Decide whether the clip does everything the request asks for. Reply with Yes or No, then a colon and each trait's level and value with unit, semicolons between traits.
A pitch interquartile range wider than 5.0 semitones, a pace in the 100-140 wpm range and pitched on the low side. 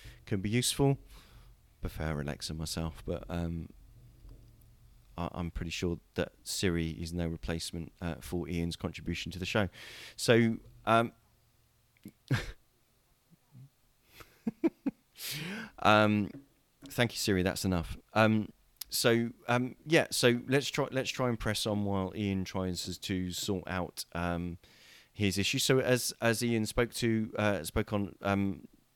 Yes: wide, 5.5 semitones; slow, 135 wpm; low, 105 Hz